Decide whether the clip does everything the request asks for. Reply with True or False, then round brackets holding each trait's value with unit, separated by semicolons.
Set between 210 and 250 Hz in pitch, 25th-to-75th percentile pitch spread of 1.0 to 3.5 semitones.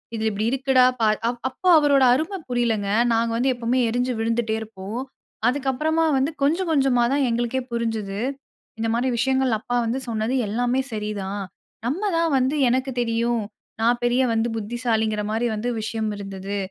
True (240 Hz; 3.0 semitones)